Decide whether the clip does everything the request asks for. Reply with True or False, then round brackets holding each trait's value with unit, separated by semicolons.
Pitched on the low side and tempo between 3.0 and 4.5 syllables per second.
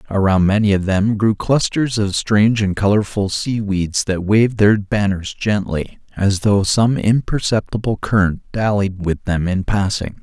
True (100 Hz; 4.4 syllables/s)